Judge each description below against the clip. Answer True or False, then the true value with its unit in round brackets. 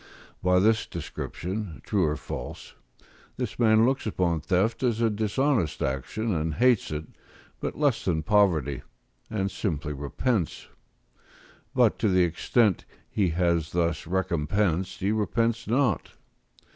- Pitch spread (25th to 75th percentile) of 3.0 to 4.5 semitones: False (4.9 semitones)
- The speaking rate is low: True (130 wpm)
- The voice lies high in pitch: False (95 Hz)